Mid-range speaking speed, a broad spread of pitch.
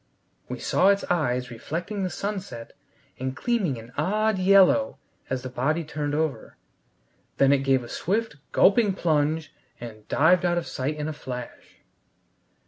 Yes: average, 150 wpm; wide, 6.5 semitones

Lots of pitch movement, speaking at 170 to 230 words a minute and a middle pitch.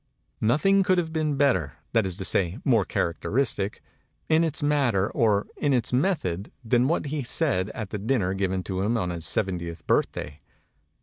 No: wide, 7.4 semitones; average, 175 wpm; low, 115 Hz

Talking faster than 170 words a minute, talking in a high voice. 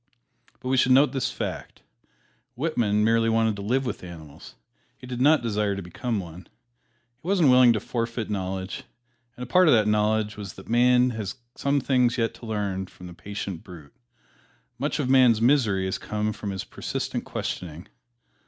No: average, 180 wpm; low, 110 Hz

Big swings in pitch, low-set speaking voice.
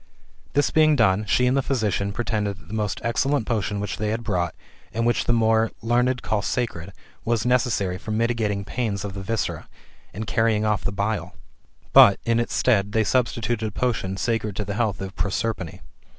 No: average, 2.7 semitones; low, 110 Hz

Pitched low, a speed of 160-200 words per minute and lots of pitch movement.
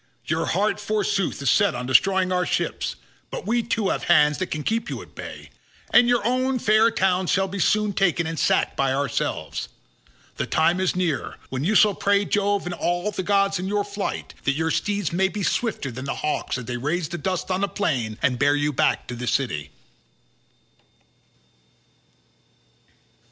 No: medium, 185 Hz; average, 185 wpm; wide, 5.7 semitones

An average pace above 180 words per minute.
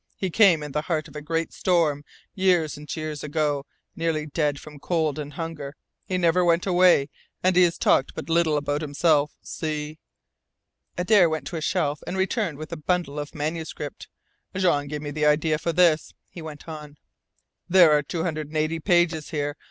Yes: average, 190 wpm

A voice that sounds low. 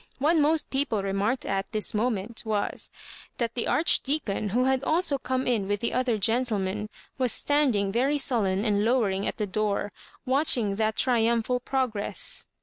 No: high, 230 Hz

